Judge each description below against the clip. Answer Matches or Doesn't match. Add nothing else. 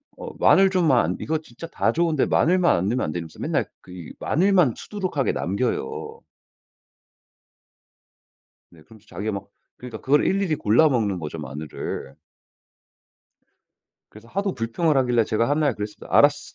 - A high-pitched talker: Doesn't match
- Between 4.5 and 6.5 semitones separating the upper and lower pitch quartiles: Doesn't match